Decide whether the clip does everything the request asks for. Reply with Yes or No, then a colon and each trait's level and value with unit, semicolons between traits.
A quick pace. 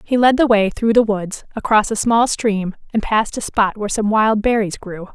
Yes: fast, 235 wpm